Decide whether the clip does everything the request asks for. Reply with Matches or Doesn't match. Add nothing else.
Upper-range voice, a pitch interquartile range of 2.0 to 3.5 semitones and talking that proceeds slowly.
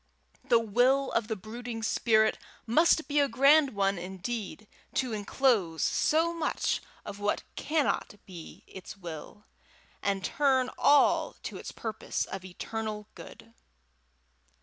Doesn't match